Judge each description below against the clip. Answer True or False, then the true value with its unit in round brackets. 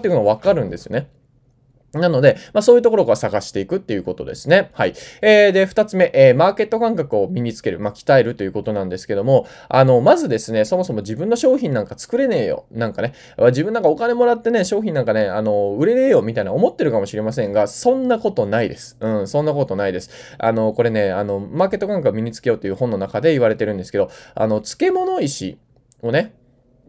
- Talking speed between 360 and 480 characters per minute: True (475 characters per minute)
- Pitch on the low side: True (130 Hz)